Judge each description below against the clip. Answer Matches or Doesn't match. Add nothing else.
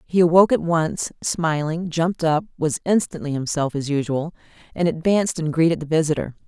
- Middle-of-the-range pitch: Matches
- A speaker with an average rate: Matches